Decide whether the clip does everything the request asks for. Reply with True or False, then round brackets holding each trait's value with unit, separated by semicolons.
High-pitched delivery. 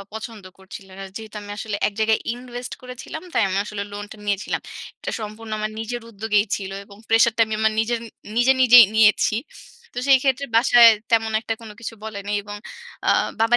True (220 Hz)